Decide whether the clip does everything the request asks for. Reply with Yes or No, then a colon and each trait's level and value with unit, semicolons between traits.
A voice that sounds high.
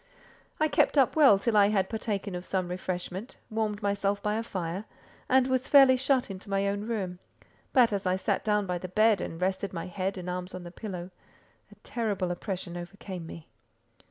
Yes: high, 200 Hz